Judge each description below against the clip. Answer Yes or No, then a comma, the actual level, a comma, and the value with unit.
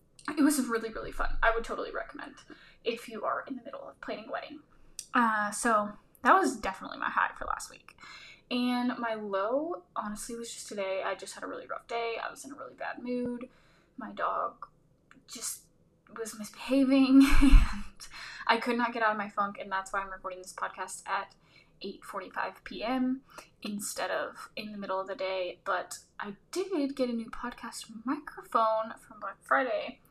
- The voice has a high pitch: Yes, high, 230 Hz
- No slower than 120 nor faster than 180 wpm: No, average, 190 wpm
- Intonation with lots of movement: No, average, 3.7 semitones